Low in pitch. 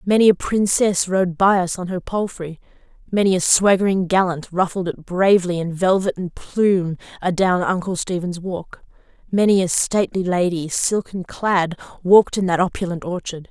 No: medium, 185 Hz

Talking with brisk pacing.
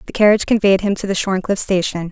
Yes: fast, 225 wpm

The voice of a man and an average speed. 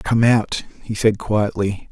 Yes: male; average, 155 wpm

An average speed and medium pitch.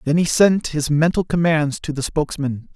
Yes: average, 195 wpm; medium, 155 Hz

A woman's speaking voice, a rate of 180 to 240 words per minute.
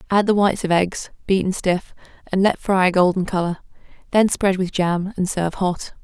Yes: female; average, 200 wpm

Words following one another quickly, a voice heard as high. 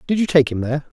No: fast, 305 wpm; medium, 145 Hz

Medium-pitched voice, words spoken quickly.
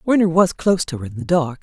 Yes: medium, 165 Hz; fast, 295 wpm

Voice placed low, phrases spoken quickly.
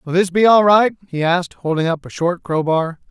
No: medium, 175 Hz; fast, 250 wpm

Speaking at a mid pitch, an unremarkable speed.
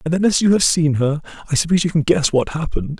No: medium, 160 Hz; fast, 280 wpm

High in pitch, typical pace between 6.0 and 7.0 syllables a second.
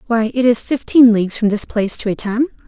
Yes: high, 230 Hz; 6.3 syllables/s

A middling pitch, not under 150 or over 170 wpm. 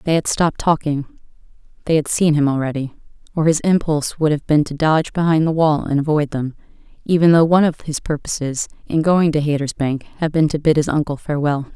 No: medium, 155 Hz; fast, 205 wpm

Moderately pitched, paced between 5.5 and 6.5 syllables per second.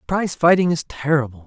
Yes: medium, 155 Hz; 6.1 syllables/s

